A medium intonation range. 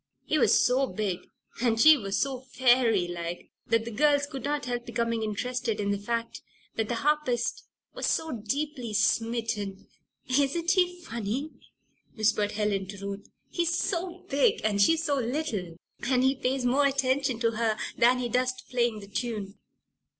Yes: average, 4.3 semitones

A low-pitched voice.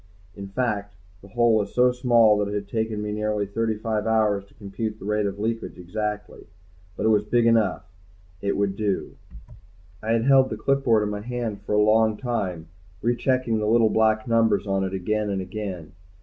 Yes: low, 105 Hz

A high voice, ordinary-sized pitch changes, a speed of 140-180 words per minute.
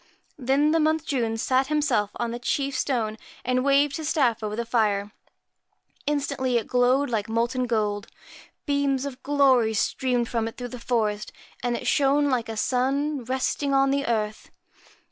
Yes: very high, 255 Hz; average, 3.4 semitones; average, 165 wpm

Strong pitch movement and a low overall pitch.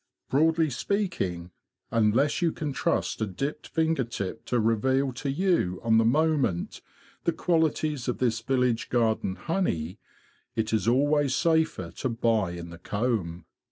Yes: wide, 5.9 semitones; low, 125 Hz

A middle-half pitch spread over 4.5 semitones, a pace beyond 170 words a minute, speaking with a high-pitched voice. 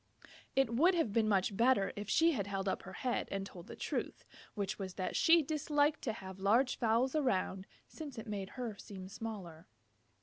Yes: average, 5.3 semitones; average, 195 wpm; high, 215 Hz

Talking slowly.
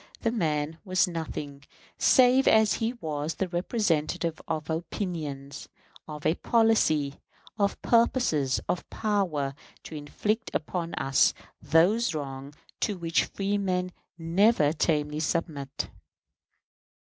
Yes: slow, 110 wpm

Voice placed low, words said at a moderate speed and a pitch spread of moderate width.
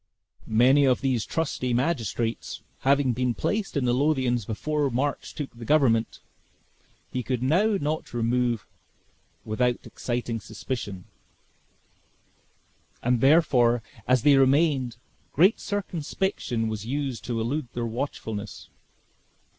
No: low, 125 Hz; slow, 115 wpm; average, 3.6 semitones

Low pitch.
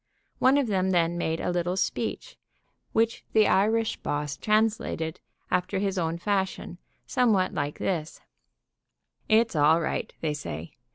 No: medium, 185 Hz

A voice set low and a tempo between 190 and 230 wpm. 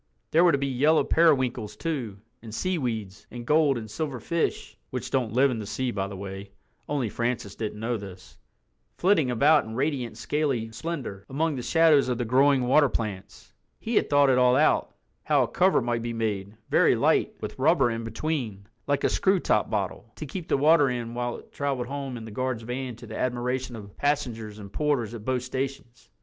Yes: low, 125 Hz; average, 200 wpm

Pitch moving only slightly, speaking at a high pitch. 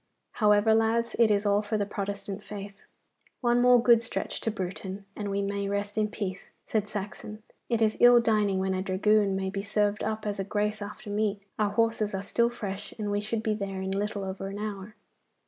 Yes: narrow, 1.5 semitones; high, 205 Hz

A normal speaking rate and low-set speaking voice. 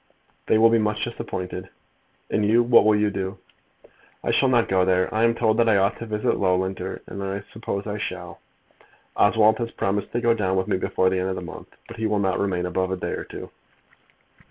No: fast, 225 wpm; low, 100 Hz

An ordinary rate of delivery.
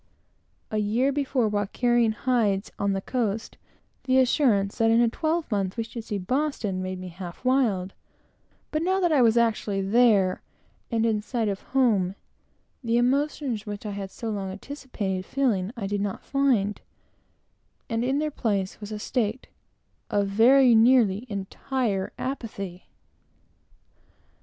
Yes: average, 145 wpm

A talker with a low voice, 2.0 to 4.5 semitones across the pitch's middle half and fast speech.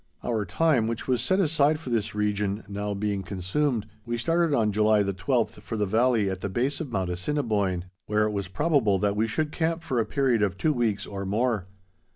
No: low, 110 Hz; average, 4.9 semitones; fast, 210 wpm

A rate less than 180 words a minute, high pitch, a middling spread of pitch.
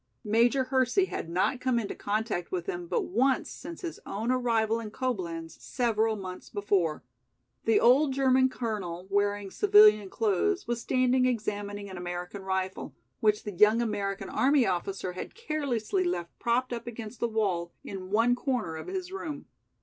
Yes: average, 160 wpm; high, 220 Hz; average, 4.7 semitones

